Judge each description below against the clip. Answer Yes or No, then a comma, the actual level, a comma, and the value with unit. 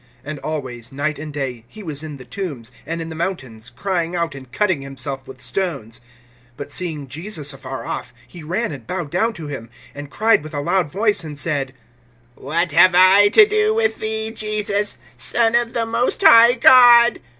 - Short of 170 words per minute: No, average, 190 wpm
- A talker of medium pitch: Yes, medium, 165 Hz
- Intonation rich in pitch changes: Yes, wide, 7.1 semitones